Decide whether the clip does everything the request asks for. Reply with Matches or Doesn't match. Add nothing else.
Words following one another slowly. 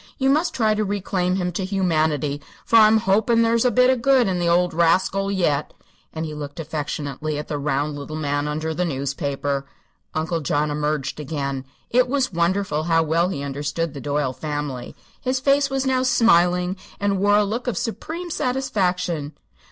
Doesn't match